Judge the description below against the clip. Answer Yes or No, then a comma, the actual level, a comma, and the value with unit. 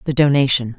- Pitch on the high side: No, low, 130 Hz